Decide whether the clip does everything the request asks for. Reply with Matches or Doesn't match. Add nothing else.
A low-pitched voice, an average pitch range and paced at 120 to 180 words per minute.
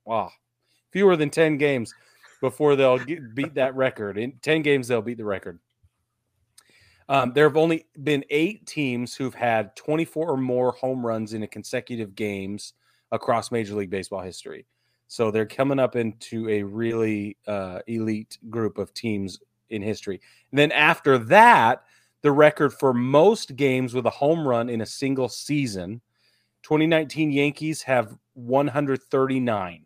Matches